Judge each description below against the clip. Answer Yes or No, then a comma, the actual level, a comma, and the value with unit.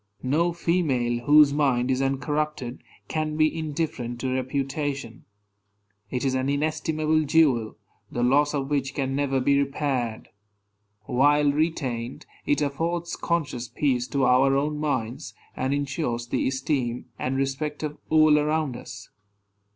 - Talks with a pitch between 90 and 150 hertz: Yes, medium, 140 Hz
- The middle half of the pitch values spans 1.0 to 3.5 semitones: Yes, average, 2.9 semitones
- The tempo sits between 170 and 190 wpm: No, slow, 135 wpm